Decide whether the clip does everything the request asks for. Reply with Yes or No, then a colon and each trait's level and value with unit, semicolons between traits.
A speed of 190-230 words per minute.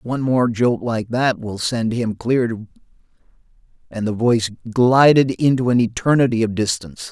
No: average, 160 wpm